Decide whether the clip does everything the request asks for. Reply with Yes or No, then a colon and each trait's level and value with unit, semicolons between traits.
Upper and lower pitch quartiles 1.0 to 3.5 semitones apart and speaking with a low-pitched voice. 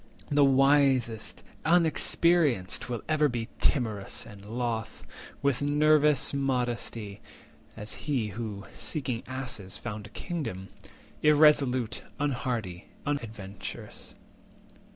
No: average, 5.0 semitones; low, 125 Hz